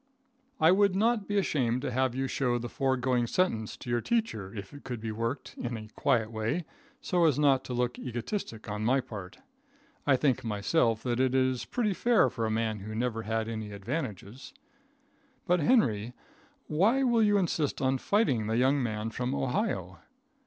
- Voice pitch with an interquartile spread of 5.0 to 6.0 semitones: Yes, average, 5.3 semitones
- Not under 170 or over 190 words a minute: Yes, average, 180 wpm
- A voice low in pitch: Yes, low, 125 Hz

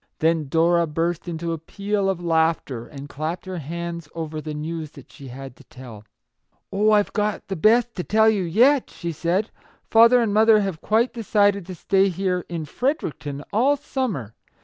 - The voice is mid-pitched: Yes, medium, 175 Hz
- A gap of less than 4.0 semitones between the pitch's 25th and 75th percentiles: No, average, 5.0 semitones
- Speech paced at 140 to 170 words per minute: No, average, 190 wpm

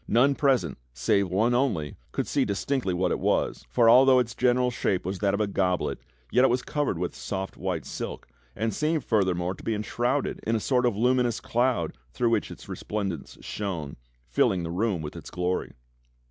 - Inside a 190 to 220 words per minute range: Yes, average, 200 wpm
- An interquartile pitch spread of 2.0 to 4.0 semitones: No, average, 5.2 semitones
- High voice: No, low, 110 Hz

